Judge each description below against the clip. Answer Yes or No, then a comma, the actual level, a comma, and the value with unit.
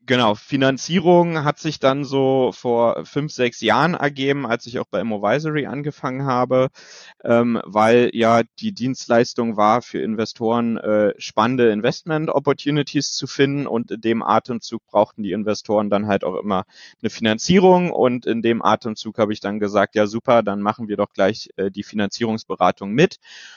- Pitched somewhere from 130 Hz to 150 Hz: No, low, 120 Hz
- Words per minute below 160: No, average, 165 wpm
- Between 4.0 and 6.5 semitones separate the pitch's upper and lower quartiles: Yes, average, 4.3 semitones